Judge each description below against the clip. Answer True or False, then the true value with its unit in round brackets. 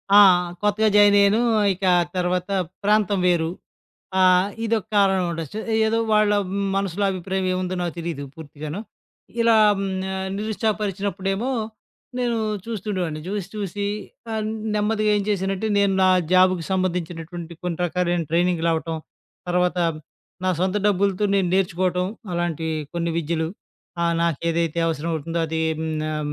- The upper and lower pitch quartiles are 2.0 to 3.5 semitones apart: True (3.1 semitones)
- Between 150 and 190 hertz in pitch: True (185 Hz)